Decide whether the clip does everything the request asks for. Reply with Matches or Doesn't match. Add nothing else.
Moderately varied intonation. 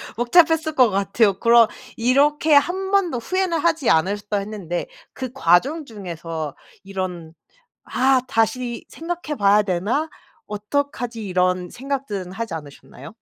Doesn't match